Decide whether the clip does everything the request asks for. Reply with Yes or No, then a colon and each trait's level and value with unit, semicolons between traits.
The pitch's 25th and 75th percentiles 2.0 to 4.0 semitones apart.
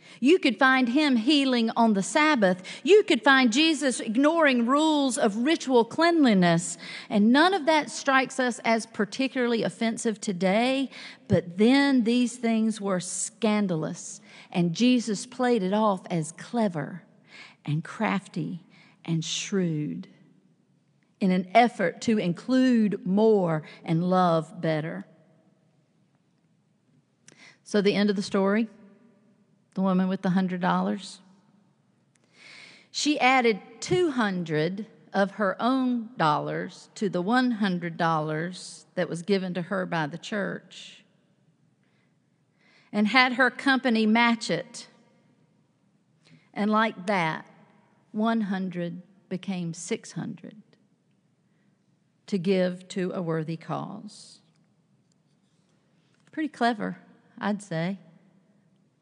No: average, 4.6 semitones